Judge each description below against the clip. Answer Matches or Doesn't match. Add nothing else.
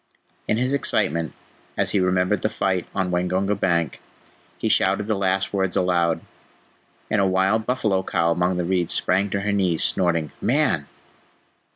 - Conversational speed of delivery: Matches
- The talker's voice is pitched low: Matches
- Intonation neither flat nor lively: Doesn't match